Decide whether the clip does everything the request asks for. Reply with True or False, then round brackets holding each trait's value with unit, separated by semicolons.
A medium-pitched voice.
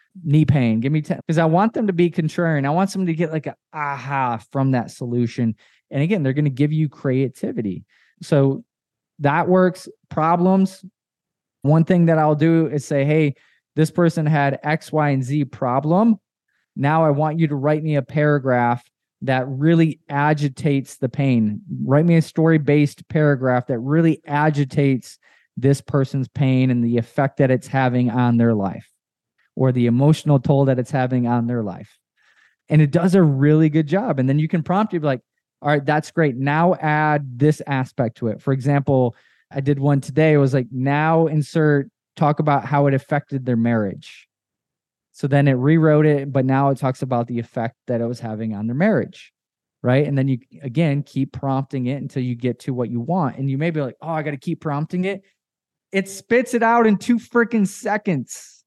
True (145 Hz)